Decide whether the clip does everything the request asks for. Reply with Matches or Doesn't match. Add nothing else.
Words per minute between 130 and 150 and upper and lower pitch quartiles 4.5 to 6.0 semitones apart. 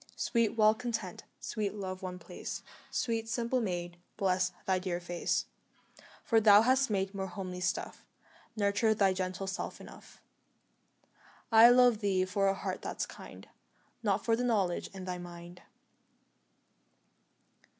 Doesn't match